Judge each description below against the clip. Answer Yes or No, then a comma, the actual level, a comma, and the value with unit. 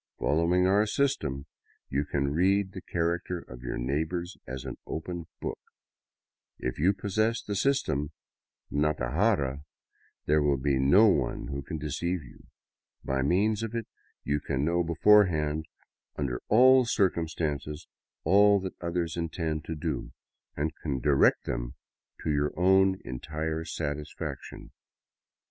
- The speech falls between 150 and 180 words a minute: No, slow, 135 wpm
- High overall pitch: No, very low, 80 Hz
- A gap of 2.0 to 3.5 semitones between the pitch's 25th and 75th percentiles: No, average, 4.7 semitones